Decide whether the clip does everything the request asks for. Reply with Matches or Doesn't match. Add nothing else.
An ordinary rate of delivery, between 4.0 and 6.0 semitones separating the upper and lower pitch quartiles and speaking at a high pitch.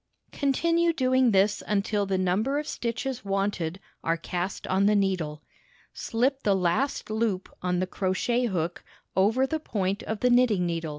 Matches